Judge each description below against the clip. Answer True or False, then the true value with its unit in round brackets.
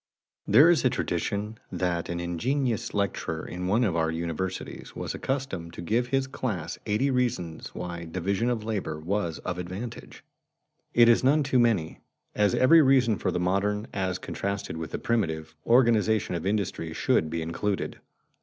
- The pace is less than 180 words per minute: True (170 wpm)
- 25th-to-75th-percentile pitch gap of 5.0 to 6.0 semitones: True (5.6 semitones)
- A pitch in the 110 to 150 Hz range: False (100 Hz)